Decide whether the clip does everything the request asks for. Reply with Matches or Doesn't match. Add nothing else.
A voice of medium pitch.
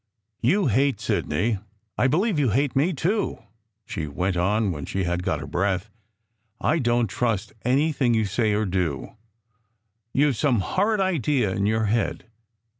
Doesn't match